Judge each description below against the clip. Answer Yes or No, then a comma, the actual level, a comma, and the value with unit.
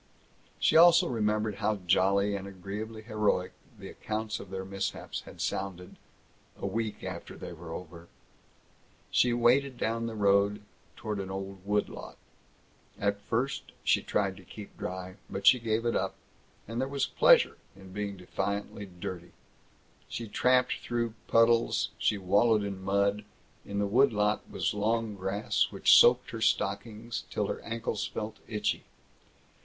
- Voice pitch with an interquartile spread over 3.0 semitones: No, average, 2.7 semitones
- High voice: No, low, 105 Hz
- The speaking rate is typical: Yes, average, 155 wpm